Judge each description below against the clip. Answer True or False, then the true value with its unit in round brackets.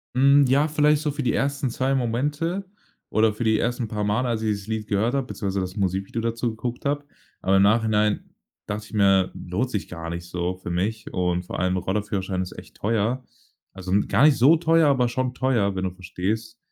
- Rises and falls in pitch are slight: False (5.1 semitones)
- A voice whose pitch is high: False (110 Hz)